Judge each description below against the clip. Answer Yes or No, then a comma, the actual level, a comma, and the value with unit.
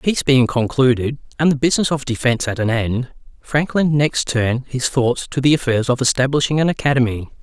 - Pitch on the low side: Yes, low, 130 Hz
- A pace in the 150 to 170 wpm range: No, average, 185 wpm